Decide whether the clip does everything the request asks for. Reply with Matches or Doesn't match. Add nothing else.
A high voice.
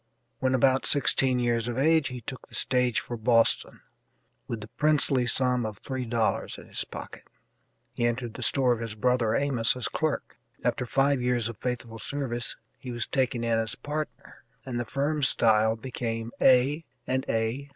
Doesn't match